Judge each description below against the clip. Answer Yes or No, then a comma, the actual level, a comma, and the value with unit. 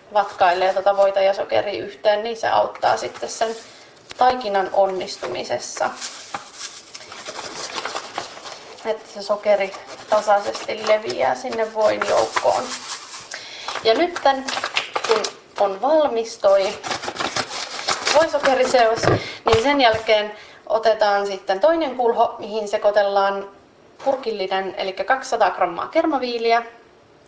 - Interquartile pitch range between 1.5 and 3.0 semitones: No, average, 3.6 semitones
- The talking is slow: Yes, slow, 90 wpm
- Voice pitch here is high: Yes, high, 215 Hz